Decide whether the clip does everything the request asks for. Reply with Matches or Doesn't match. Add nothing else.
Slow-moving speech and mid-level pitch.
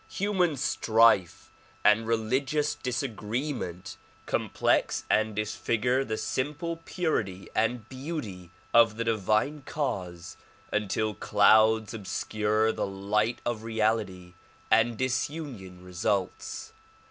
Doesn't match